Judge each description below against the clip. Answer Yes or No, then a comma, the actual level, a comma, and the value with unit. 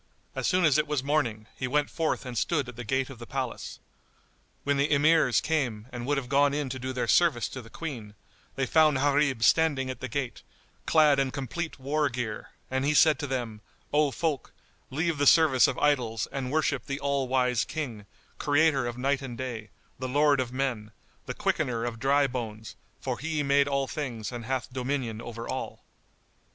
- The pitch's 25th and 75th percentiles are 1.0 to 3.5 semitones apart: Yes, average, 3.0 semitones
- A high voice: No, low, 135 Hz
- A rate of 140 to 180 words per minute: No, average, 195 wpm